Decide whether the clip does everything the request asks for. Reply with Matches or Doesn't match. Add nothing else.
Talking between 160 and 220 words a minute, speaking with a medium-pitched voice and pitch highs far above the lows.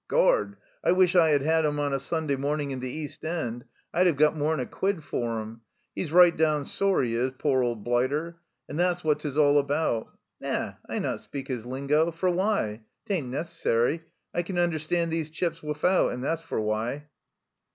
Doesn't match